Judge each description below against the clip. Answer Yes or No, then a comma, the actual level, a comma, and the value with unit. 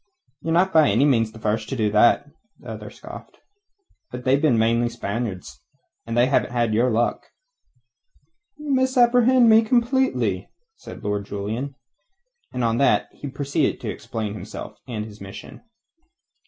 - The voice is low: Yes, low, 120 Hz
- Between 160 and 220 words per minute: No, average, 150 wpm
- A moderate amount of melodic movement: No, wide, 6.5 semitones